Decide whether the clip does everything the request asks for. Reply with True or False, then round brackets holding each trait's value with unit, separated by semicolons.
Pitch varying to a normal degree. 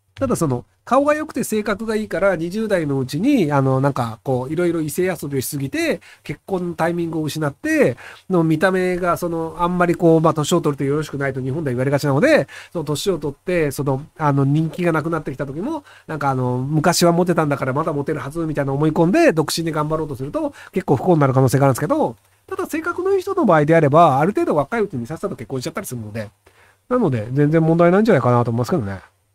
True (4.3 semitones)